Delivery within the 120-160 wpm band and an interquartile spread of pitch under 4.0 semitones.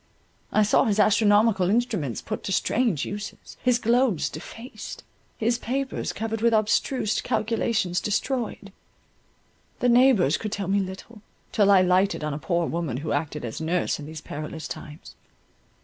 No: average, 150 wpm; average, 5.3 semitones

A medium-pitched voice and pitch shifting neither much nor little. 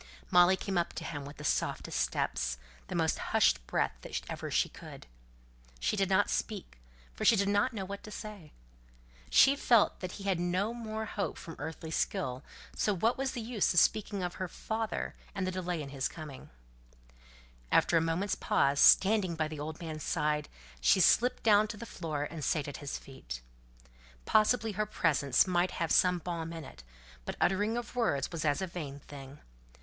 No: medium, 175 Hz; wide, 5.7 semitones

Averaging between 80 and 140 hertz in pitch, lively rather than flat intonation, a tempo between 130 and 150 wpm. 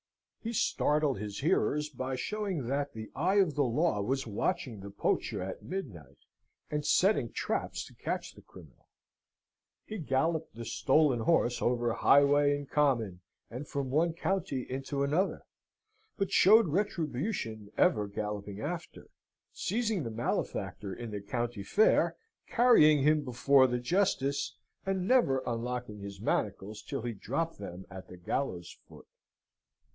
Yes: low, 135 Hz; wide, 6.3 semitones; average, 140 wpm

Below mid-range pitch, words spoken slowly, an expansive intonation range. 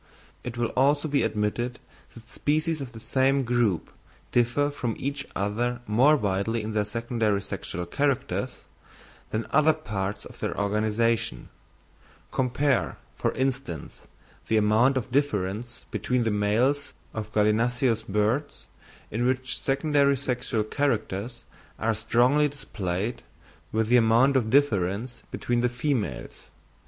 No: low, 120 Hz; slow, 130 wpm; average, 4.0 semitones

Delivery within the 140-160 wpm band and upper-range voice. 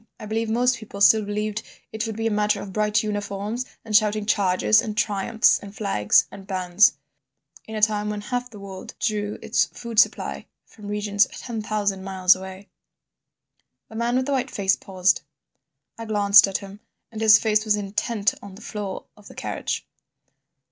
No: average, 175 wpm; high, 210 Hz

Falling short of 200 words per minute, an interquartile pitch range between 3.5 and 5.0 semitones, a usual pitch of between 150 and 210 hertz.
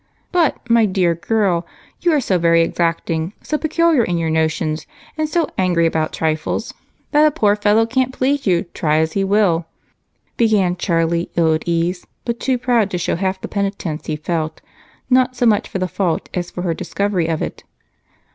No: average, 185 wpm; wide, 5.5 semitones; medium, 185 Hz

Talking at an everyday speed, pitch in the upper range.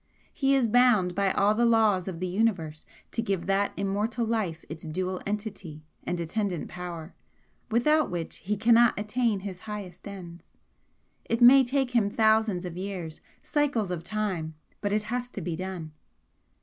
Yes: average, 160 wpm; high, 200 Hz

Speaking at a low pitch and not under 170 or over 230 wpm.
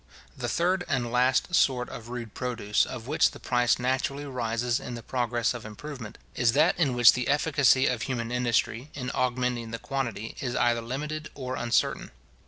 Yes: low, 125 Hz; average, 180 wpm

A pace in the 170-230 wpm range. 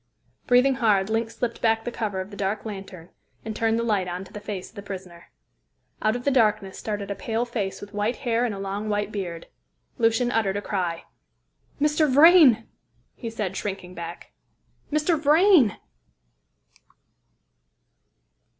No: average, 160 wpm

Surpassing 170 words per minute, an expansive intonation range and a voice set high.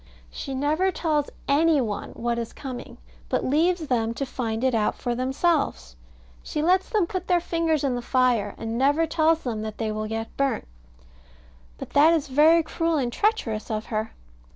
Yes: average, 180 wpm; wide, 6.0 semitones; very high, 275 Hz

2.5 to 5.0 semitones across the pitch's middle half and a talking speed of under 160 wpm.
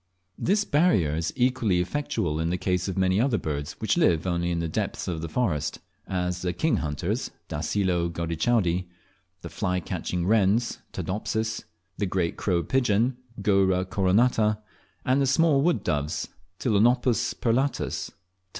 No: wide, 5.6 semitones; average, 145 wpm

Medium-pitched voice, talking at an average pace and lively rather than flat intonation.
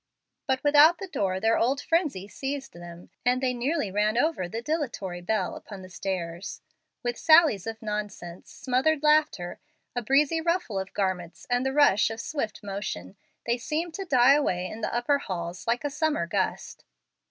No: high, 235 Hz; average, 175 wpm; wide, 7.3 semitones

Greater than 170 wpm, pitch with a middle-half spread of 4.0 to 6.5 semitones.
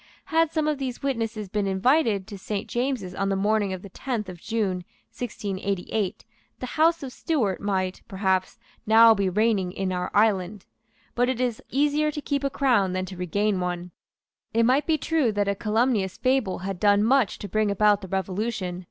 Yes: average, 185 wpm; average, 4.8 semitones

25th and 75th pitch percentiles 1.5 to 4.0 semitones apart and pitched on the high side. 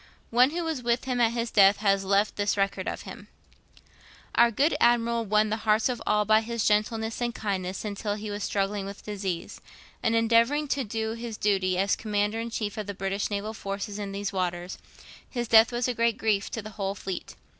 Yes: narrow, 2.6 semitones; high, 215 Hz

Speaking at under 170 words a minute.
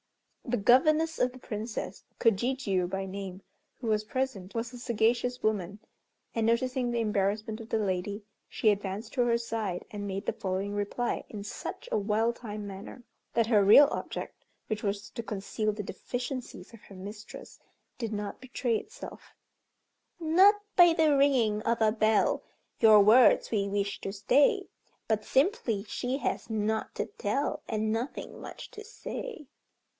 Yes: average, 160 wpm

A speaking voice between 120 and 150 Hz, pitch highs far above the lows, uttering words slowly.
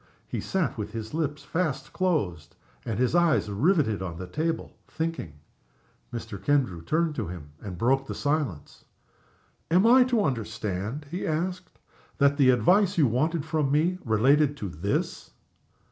No: medium, 140 Hz; wide, 7.3 semitones; average, 150 wpm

